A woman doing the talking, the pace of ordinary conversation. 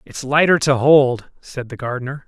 No: male; average, 185 wpm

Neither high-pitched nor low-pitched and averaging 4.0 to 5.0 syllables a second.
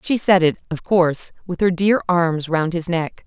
Yes: medium, 175 Hz; 4.6 syllables/s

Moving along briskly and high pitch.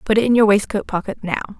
Yes: fast, 265 wpm; high, 210 Hz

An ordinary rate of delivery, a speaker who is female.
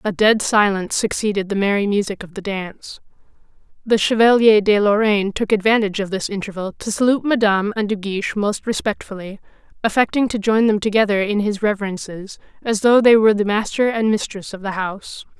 Yes: average, 180 wpm; female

